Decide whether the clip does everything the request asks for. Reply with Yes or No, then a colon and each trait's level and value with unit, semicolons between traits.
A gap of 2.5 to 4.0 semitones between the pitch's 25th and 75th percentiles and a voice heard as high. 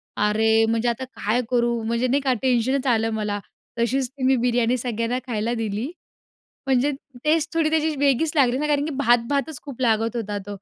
Yes: average, 3.2 semitones; high, 245 Hz